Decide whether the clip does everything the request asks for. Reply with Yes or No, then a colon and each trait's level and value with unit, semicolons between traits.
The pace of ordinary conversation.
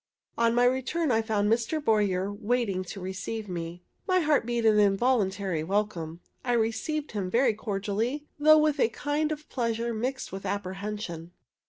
Yes: average, 160 wpm